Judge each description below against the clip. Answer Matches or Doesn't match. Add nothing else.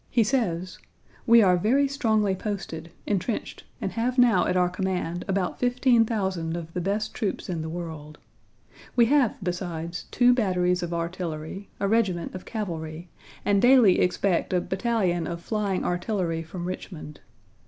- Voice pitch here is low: Doesn't match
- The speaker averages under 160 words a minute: Matches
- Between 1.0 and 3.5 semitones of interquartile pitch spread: Doesn't match